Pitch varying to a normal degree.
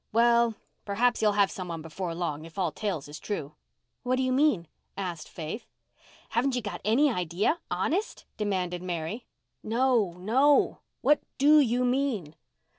No: wide, 6.2 semitones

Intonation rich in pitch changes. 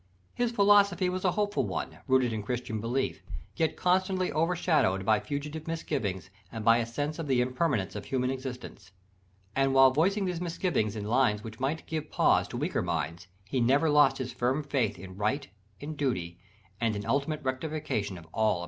Yes: wide, 6.4 semitones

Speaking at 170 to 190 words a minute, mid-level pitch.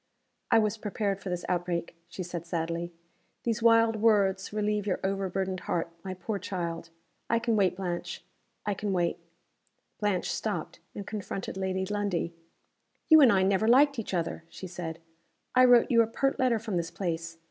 No: average, 175 wpm; high, 195 Hz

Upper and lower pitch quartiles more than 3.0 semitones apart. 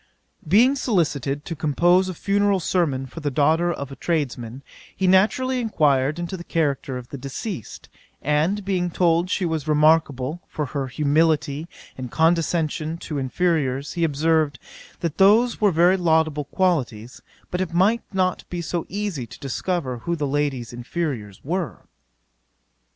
Yes: average, 4.3 semitones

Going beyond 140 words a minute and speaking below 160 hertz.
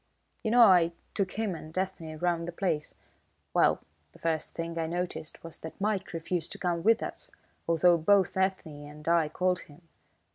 No: average, 180 wpm; medium, 170 Hz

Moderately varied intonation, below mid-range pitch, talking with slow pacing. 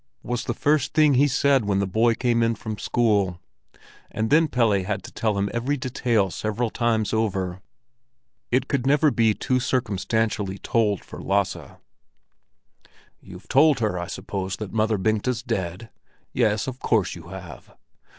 No: average, 3.7 semitones; low, 110 Hz; average, 160 wpm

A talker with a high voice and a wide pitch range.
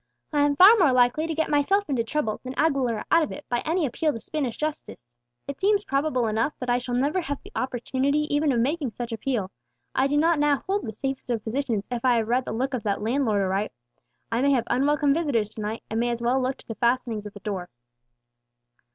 No: very high, 255 Hz; average, 4.2 semitones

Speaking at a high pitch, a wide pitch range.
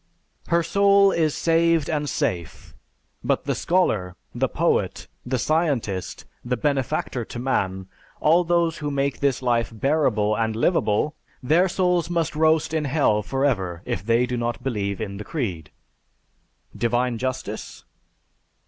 No: low, 130 Hz; wide, 6.4 semitones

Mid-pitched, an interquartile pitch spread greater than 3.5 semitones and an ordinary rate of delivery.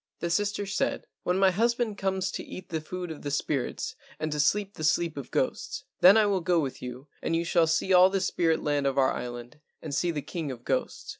No: medium, 170 Hz; average, 4.5 semitones; fast, 235 wpm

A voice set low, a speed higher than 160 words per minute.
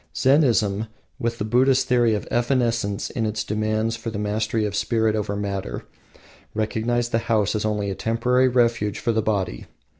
Yes: low, 110 Hz; average, 170 wpm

